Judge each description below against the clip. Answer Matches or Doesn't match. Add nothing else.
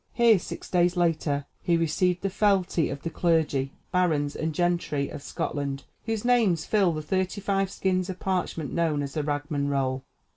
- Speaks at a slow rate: Doesn't match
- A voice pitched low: Doesn't match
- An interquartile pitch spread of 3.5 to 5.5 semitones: Matches